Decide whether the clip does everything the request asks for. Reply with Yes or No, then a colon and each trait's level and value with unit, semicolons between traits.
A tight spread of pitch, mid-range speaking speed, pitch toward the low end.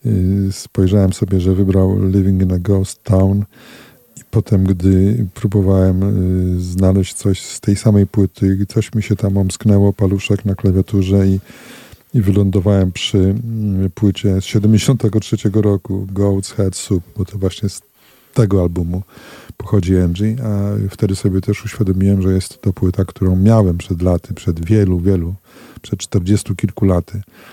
Yes: narrow, 1.7 semitones; average, 145 wpm; low, 100 Hz